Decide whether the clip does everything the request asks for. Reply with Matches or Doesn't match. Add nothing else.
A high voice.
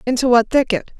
Matches